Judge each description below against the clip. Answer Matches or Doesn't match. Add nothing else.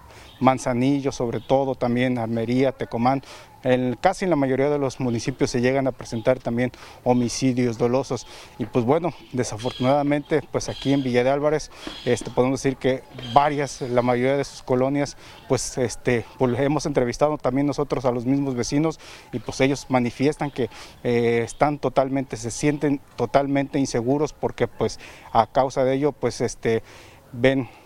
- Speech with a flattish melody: Matches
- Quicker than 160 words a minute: Doesn't match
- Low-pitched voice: Matches